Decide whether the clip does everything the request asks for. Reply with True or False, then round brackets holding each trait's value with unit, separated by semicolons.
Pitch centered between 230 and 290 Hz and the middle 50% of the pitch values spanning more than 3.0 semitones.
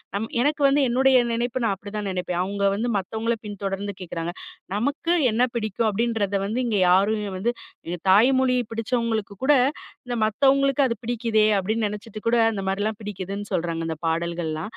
False (215 Hz; 3.4 semitones)